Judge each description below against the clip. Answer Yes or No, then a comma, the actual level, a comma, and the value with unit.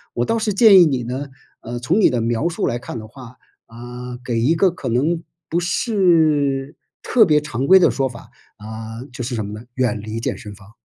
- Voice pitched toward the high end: No, low, 125 Hz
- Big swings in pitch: Yes, wide, 5.8 semitones